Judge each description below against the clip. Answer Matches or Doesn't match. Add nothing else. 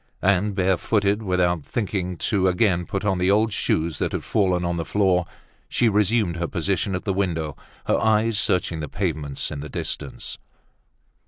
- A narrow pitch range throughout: Doesn't match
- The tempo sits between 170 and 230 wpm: Matches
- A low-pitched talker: Matches